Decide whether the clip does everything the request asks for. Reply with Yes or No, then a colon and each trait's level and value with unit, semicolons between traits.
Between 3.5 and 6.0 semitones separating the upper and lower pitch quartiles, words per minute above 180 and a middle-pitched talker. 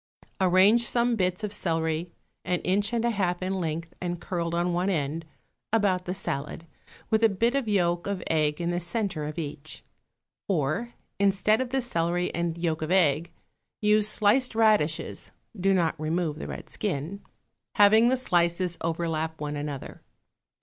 No: average, 4.1 semitones; average, 165 wpm; medium, 180 Hz